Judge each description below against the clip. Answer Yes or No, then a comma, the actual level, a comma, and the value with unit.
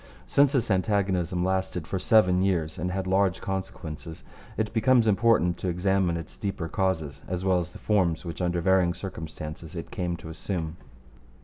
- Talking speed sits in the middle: Yes, average, 170 wpm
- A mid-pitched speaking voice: No, very low, 90 Hz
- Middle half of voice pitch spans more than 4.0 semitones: No, narrow, 2.5 semitones